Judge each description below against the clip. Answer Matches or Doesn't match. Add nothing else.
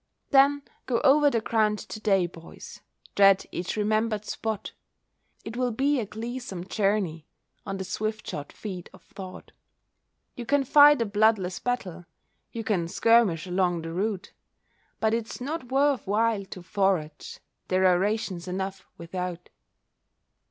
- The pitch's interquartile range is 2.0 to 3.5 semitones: Doesn't match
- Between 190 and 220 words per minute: Doesn't match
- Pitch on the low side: Doesn't match